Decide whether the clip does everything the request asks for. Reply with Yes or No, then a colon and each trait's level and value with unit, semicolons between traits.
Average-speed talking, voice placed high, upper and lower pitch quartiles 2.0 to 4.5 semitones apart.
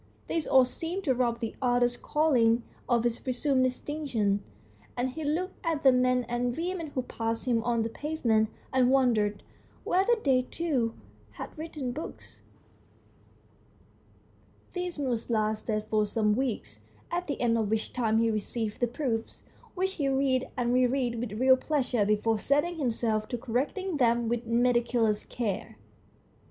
Yes: average, 155 wpm; high, 245 Hz; average, 3.7 semitones